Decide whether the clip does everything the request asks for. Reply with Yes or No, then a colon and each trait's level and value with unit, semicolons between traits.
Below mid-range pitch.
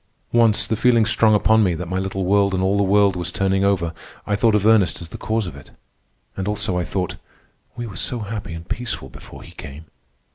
Yes: low, 100 Hz